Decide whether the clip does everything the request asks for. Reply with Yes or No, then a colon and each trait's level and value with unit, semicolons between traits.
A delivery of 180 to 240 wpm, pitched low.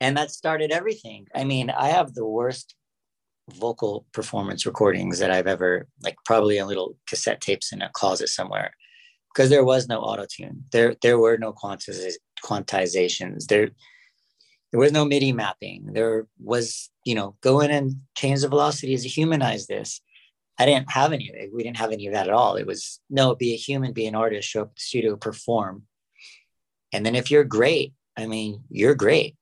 Yes: average, 185 wpm; low, 125 Hz